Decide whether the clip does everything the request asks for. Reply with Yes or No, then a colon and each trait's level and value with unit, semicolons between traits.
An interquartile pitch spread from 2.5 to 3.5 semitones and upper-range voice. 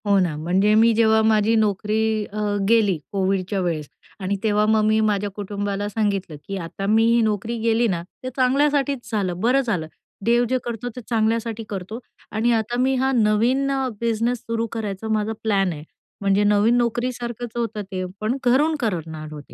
Yes: average, 3.0 semitones; high, 220 Hz